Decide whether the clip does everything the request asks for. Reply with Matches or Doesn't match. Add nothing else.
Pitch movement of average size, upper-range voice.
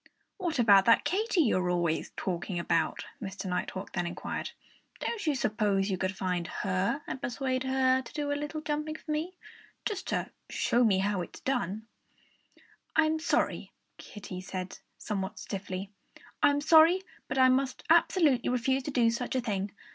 Doesn't match